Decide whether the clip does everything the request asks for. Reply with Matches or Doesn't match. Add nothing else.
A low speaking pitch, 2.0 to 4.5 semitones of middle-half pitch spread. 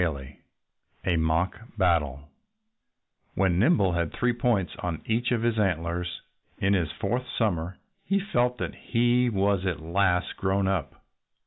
Doesn't match